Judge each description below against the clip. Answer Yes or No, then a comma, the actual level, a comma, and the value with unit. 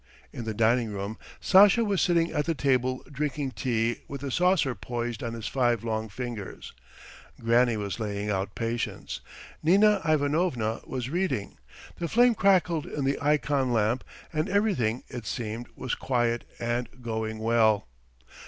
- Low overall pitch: Yes, low, 125 Hz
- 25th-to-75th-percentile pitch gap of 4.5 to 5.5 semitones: Yes, average, 5.1 semitones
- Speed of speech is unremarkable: Yes, average, 150 wpm